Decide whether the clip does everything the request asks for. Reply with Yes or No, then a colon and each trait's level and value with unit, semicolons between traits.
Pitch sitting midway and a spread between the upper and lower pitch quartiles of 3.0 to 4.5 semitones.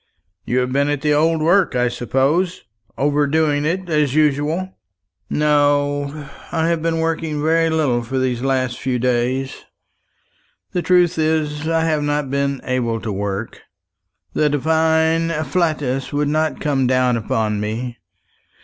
Yes: medium, 145 Hz; average, 3.8 semitones